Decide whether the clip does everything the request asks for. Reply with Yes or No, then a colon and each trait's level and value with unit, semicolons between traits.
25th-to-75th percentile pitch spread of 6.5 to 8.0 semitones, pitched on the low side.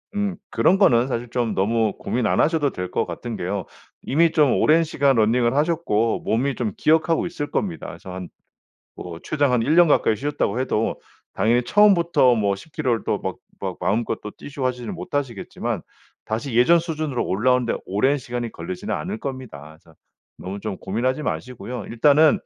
No: wide, 5.4 semitones; low, 125 Hz